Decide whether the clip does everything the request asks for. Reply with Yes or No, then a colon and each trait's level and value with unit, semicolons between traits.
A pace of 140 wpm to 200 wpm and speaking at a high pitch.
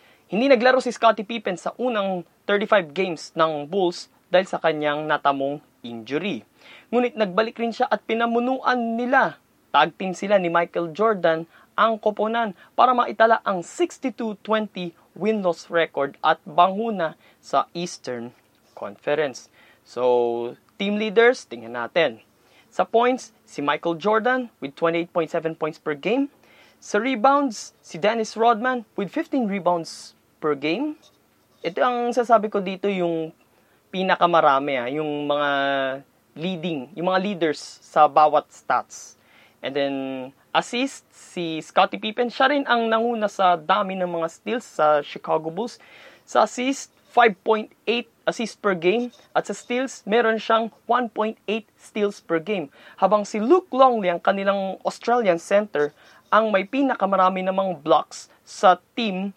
No: average, 130 wpm; high, 195 Hz